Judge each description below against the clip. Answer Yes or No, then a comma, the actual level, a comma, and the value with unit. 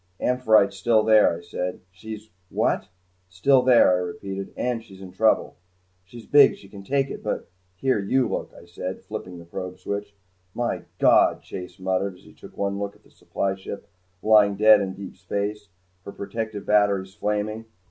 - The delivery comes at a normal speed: Yes, average, 180 wpm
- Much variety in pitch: No, narrow, 2.5 semitones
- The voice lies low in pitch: Yes, low, 100 Hz